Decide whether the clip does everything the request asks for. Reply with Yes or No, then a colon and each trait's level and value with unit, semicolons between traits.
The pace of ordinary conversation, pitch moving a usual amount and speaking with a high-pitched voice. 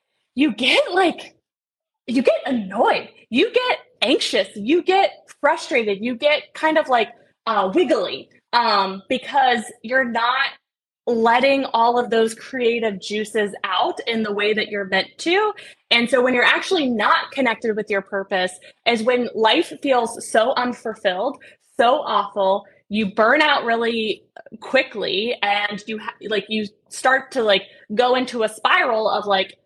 Yes: average, 150 wpm; average, 4.0 semitones; high, 235 Hz